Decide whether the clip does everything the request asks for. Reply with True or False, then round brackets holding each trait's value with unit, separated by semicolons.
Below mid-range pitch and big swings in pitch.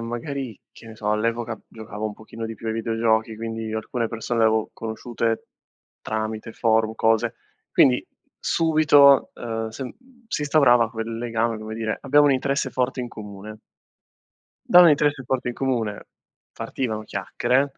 False (115 Hz; 2.6 semitones)